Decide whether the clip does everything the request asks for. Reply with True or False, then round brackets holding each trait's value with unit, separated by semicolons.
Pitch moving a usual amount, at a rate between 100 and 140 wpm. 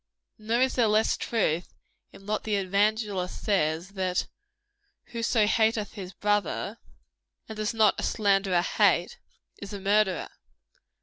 False (2.3 semitones; 135 wpm)